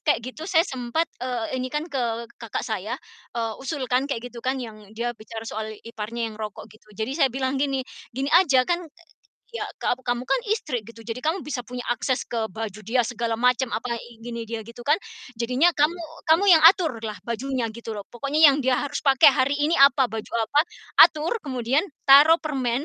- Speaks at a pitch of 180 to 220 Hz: No, very high, 250 Hz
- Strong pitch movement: No, average, 3.8 semitones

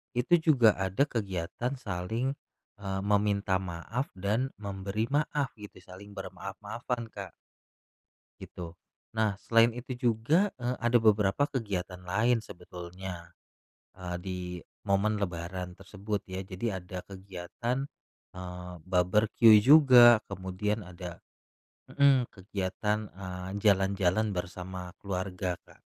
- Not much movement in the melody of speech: No, average, 3.8 semitones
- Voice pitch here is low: Yes, low, 100 Hz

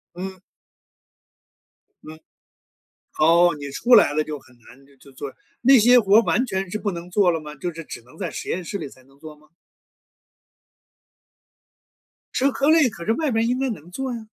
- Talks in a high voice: No, medium, 180 Hz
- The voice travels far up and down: Yes, wide, 7.0 semitones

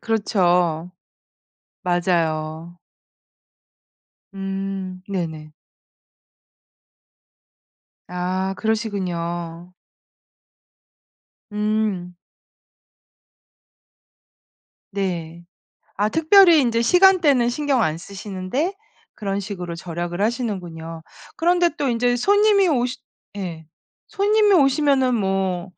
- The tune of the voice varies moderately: No, wide, 6.3 semitones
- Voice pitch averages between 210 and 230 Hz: No, high, 195 Hz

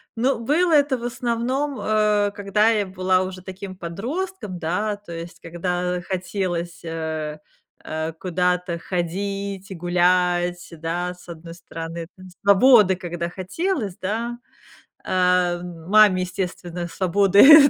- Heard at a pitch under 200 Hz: Yes, medium, 185 Hz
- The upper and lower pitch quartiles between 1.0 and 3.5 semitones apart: Yes, average, 3.1 semitones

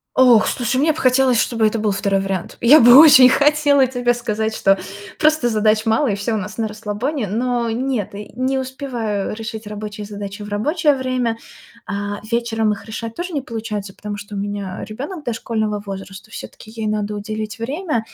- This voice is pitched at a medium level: No, high, 225 Hz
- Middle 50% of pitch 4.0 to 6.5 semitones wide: No, average, 3.6 semitones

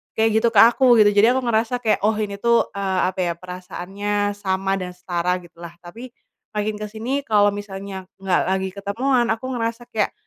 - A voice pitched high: Yes, high, 205 Hz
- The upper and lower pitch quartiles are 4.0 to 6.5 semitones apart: No, average, 3.1 semitones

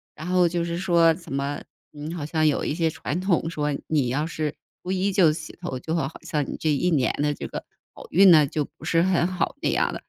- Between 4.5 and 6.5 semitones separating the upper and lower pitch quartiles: No, average, 2.8 semitones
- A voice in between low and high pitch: Yes, medium, 160 Hz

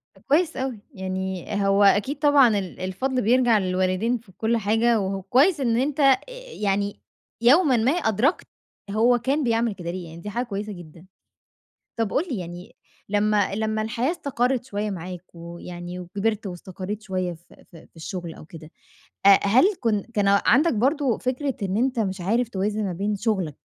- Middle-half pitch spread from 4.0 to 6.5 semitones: Yes, average, 4.7 semitones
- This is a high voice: Yes, high, 210 Hz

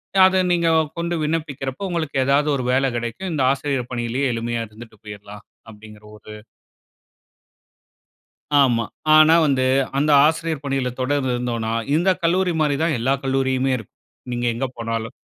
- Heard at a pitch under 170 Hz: Yes, low, 135 Hz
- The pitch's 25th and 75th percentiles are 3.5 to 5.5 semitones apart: Yes, average, 4.9 semitones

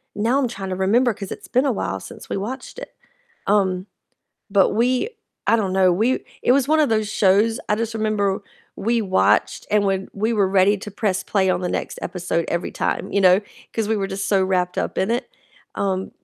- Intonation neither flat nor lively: Yes, average, 3.0 semitones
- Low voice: No, high, 200 Hz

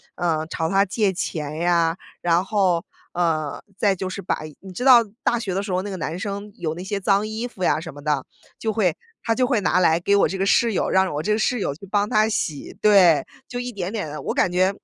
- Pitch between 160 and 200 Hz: Yes, high, 190 Hz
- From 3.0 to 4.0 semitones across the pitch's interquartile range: Yes, average, 3.7 semitones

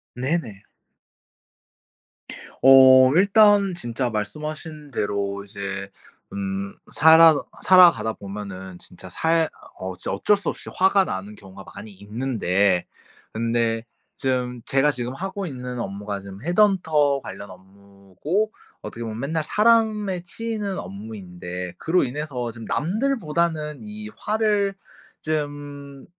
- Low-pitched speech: Yes, low, 130 Hz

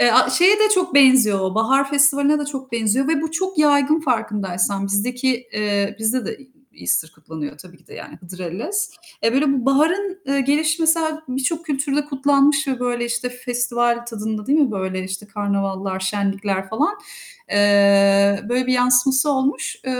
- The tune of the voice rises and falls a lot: Yes, wide, 6.1 semitones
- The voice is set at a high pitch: Yes, very high, 250 Hz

